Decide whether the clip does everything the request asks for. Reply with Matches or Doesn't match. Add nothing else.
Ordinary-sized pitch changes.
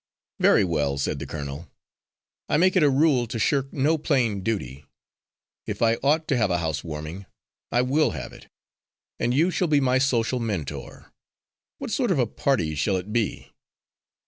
Doesn't match